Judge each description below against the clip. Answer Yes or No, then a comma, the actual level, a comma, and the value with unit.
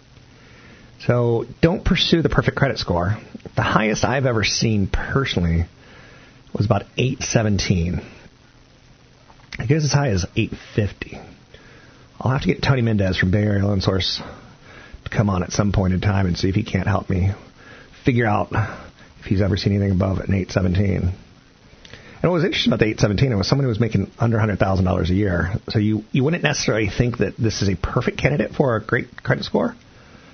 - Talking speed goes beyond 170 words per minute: Yes, average, 195 wpm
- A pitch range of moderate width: Yes, average, 4.4 semitones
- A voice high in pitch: No, low, 105 Hz